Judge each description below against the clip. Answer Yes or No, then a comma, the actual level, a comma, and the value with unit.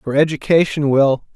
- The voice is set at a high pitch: No, medium, 145 Hz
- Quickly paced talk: No, slow, 135 wpm